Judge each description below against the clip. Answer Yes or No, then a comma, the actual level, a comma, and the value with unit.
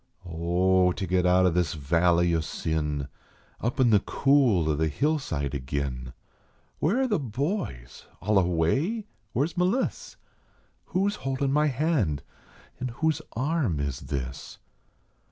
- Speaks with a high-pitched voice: No, very low, 95 Hz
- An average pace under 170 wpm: Yes, average, 145 wpm